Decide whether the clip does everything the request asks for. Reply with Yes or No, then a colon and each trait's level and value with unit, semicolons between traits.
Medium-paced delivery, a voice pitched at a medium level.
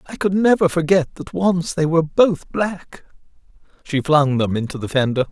Yes: average, 180 wpm; medium, 165 Hz